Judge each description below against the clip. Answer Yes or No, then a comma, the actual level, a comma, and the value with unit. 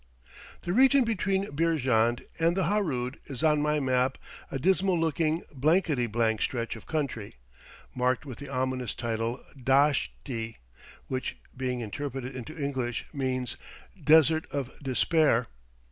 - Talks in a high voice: No, low, 135 Hz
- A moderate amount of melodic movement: Yes, average, 4.2 semitones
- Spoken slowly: Yes, slow, 130 wpm